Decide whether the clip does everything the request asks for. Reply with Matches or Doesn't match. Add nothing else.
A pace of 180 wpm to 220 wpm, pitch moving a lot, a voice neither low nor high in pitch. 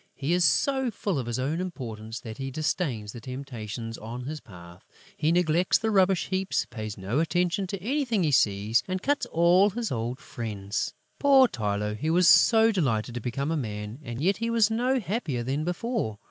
Matches